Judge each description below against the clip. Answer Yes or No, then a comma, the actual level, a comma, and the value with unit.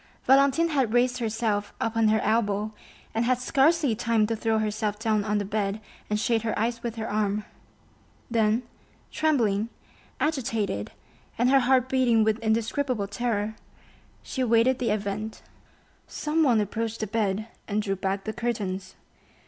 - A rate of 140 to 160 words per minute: Yes, average, 150 wpm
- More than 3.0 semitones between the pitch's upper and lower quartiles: No, narrow, 2.5 semitones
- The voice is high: Yes, high, 225 Hz